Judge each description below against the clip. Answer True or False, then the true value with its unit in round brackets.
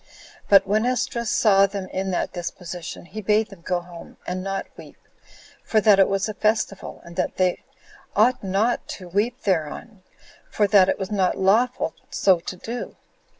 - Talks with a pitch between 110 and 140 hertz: False (195 Hz)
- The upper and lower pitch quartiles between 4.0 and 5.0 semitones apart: False (2.7 semitones)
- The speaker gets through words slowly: False (175 wpm)